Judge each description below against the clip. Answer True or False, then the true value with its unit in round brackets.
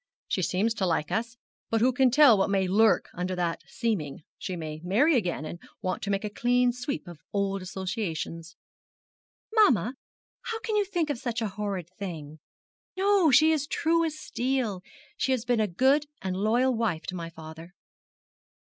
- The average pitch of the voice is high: True (215 Hz)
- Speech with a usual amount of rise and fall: False (6.2 semitones)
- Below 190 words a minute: True (180 wpm)